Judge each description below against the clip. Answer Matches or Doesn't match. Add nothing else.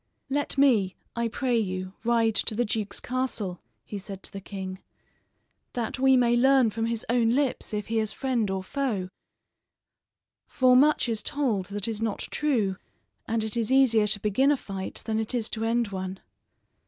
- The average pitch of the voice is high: Matches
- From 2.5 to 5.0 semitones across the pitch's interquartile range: Matches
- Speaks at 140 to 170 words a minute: Doesn't match